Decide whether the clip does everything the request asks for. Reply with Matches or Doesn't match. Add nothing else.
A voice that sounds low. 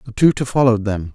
Matches